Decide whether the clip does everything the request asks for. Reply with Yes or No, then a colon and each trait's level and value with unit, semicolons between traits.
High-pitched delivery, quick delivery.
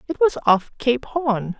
No: very high, 250 Hz; average, 190 wpm